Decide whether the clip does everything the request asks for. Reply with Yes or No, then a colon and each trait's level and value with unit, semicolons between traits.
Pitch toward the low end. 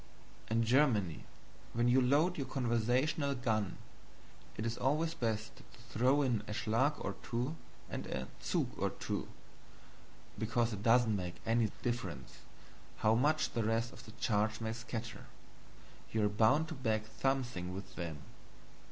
Yes: low, 115 Hz